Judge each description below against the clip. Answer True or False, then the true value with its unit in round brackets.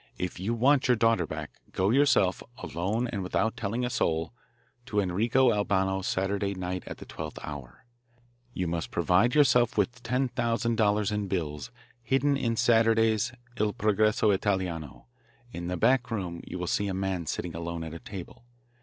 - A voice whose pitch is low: True (100 Hz)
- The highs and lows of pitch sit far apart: False (4.4 semitones)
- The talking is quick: False (165 wpm)